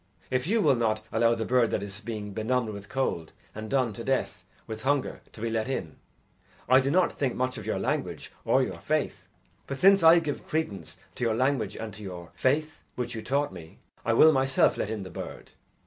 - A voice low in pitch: Yes, low, 120 Hz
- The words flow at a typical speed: No, fast, 215 wpm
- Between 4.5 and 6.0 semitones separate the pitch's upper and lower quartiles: No, average, 4.0 semitones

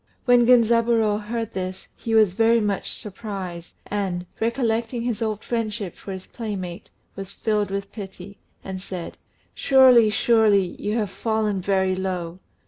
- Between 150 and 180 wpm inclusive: No, average, 140 wpm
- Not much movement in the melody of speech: No, average, 3.1 semitones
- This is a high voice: Yes, high, 210 Hz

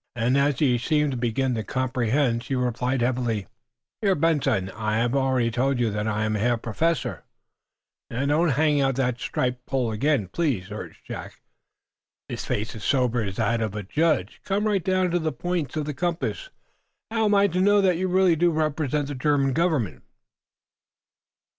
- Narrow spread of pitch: No, average, 5.3 semitones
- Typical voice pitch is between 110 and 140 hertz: Yes, low, 135 Hz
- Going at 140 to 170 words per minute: No, average, 185 wpm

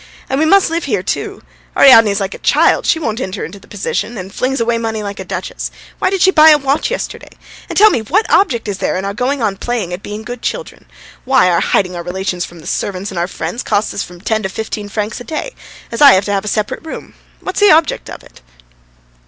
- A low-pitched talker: No, high, 220 Hz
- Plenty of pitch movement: Yes, wide, 6.2 semitones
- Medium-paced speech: No, fast, 245 wpm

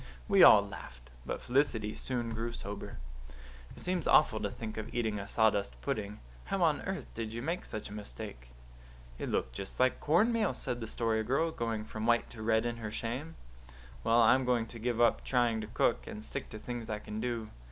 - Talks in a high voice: No, low, 115 Hz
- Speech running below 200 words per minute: No, fast, 205 wpm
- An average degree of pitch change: No, narrow, 2.3 semitones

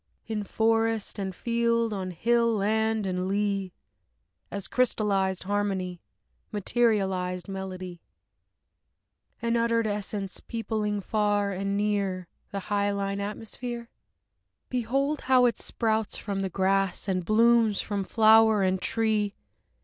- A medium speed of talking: No, slow, 110 wpm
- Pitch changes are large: No, narrow, 2.6 semitones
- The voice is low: No, high, 205 Hz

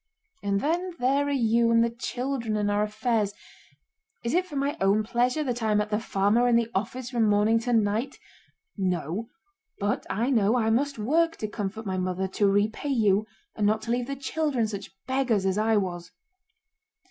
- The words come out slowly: No, average, 195 wpm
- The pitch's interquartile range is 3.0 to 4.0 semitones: Yes, average, 3.4 semitones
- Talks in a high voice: Yes, high, 225 Hz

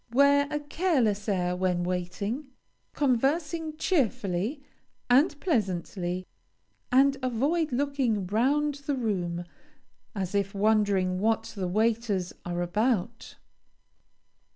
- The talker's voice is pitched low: No, high, 225 Hz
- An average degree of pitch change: No, wide, 7.0 semitones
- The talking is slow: Yes, slow, 100 wpm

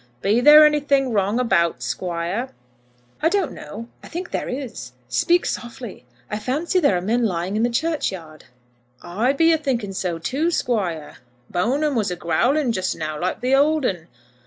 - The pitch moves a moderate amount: No, wide, 7.9 semitones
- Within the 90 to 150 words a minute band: No, average, 170 wpm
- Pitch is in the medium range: No, high, 235 Hz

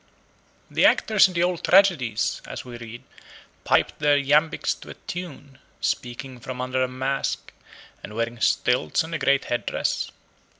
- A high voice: No, low, 135 Hz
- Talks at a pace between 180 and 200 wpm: No, average, 160 wpm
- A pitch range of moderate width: Yes, average, 4.8 semitones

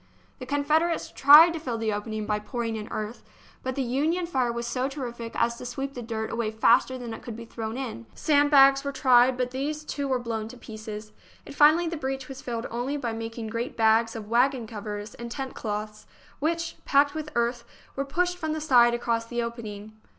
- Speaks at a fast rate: Yes, fast, 215 wpm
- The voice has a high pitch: Yes, high, 245 Hz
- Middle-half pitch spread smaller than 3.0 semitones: No, average, 3.7 semitones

